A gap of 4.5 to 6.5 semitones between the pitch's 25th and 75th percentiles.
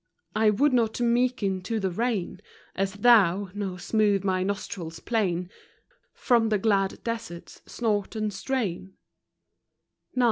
No: average, 3.3 semitones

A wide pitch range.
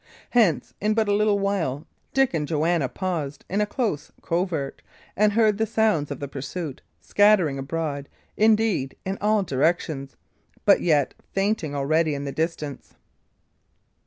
Yes: wide, 6.3 semitones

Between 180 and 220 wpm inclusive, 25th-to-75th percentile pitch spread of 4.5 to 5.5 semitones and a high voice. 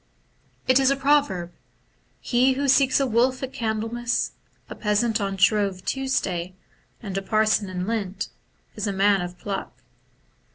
No: average, 155 wpm; average, 4.8 semitones; high, 215 Hz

